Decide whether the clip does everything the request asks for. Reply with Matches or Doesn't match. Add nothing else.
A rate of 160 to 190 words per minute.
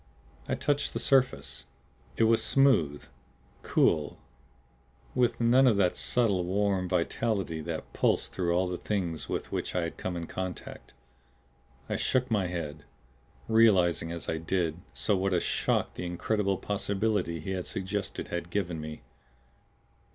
Doesn't match